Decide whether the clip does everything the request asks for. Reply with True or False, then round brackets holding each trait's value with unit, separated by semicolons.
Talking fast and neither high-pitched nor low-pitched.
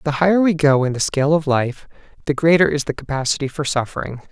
True (225 wpm; 150 Hz)